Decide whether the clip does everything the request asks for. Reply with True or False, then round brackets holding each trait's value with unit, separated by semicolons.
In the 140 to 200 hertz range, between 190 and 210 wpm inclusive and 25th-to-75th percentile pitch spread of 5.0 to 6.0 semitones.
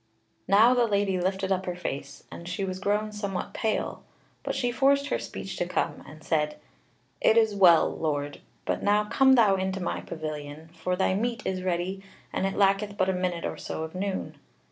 False (190 Hz; 195 wpm; 3.0 semitones)